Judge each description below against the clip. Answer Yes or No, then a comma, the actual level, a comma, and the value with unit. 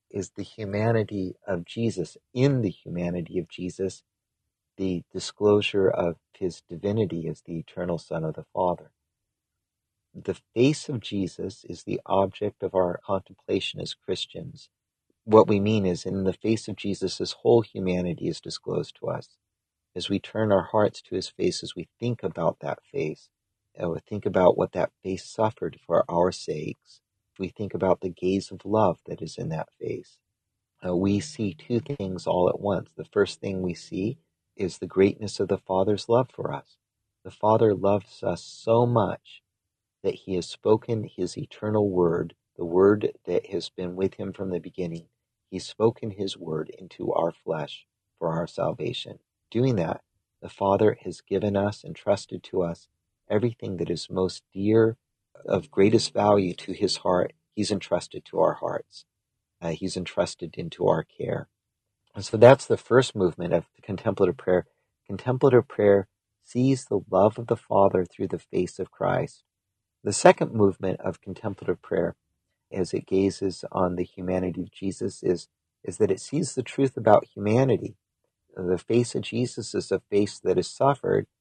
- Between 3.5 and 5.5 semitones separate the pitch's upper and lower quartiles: No, average, 3.0 semitones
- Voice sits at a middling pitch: No, low, 100 Hz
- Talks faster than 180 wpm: No, average, 170 wpm